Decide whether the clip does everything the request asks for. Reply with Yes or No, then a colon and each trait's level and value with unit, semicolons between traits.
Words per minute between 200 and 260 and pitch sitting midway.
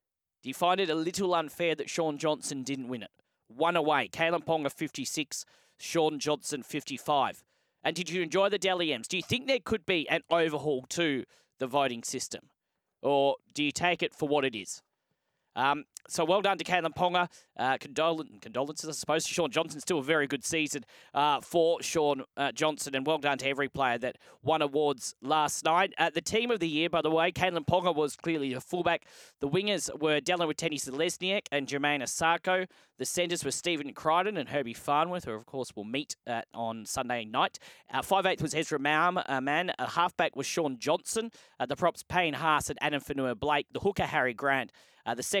Yes: fast, 205 wpm; medium, 155 Hz